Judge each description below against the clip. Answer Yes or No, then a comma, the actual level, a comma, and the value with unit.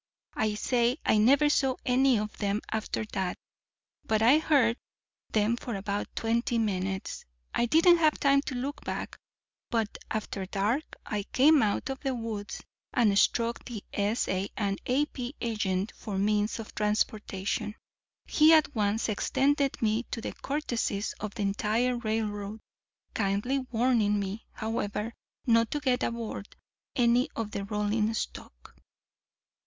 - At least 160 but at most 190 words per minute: No, average, 140 wpm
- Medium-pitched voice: No, high, 225 Hz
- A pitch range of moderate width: Yes, average, 3.3 semitones